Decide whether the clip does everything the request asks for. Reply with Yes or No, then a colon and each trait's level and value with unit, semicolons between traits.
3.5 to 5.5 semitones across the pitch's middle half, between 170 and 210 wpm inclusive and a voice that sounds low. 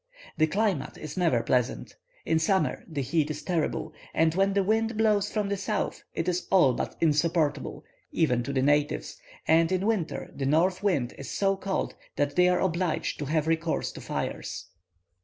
No: average, 4.5 semitones; average, 180 wpm; medium, 165 Hz